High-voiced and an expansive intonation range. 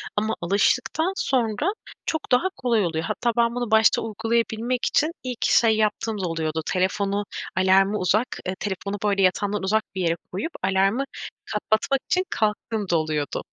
No: high, 210 Hz; average, 3.7 semitones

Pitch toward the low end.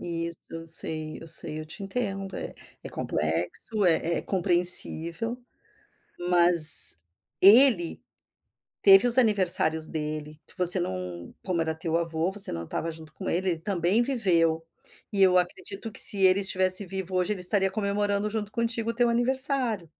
No: medium, 185 Hz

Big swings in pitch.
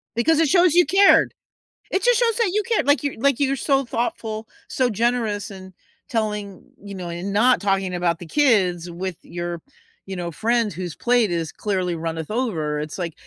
Yes: wide, 6.8 semitones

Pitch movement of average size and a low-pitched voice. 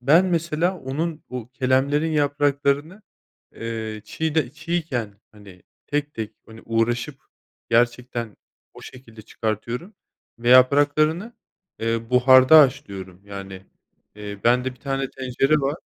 Yes: average, 4.5 semitones; low, 130 Hz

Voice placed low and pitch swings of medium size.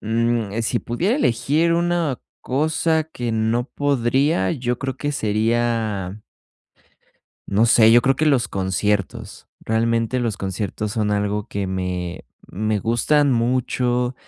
Yes: low, 115 Hz; average, 4.0 semitones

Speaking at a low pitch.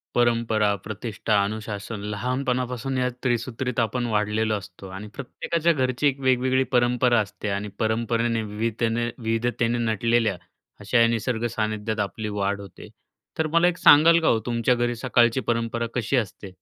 Yes: low, 115 Hz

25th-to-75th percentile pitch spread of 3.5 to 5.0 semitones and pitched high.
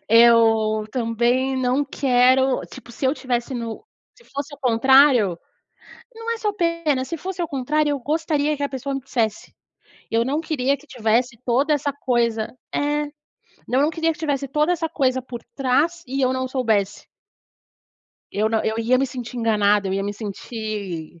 Yes: average, 4.0 semitones; very high, 260 Hz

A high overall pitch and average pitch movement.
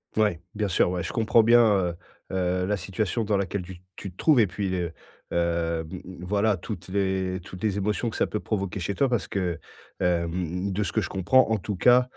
No: very low, 95 Hz; average, 3.0 semitones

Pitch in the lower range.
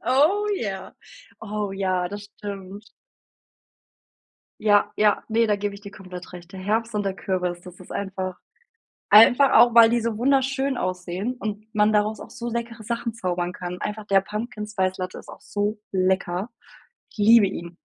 No: high, 205 Hz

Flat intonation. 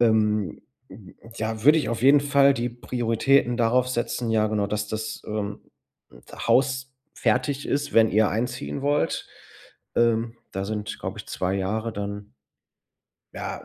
No: average, 3.1 semitones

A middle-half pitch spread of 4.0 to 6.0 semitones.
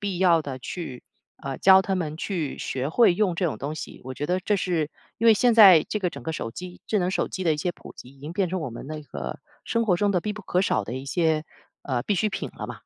Yes: average, 4.7 semitones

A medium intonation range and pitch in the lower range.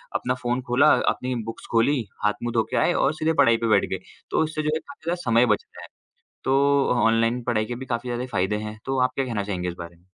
Yes: average, 3.2 semitones; low, 120 Hz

